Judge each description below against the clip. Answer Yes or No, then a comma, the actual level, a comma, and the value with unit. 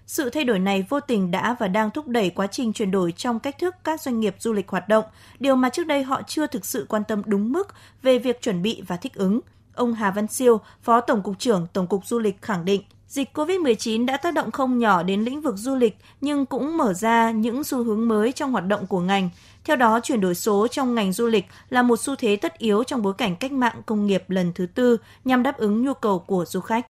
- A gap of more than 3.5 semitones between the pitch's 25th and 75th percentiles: Yes, average, 4.3 semitones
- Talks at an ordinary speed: No, fast, 260 wpm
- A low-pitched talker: No, high, 230 Hz